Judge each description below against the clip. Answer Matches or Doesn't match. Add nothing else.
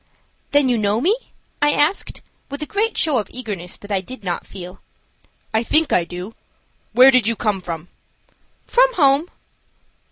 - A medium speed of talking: Matches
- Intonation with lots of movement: Matches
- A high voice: Matches